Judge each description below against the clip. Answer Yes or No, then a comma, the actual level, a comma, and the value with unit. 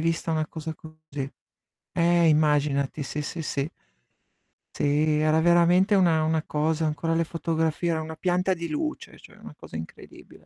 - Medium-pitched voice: Yes, medium, 160 Hz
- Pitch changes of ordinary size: No, narrow, 1.7 semitones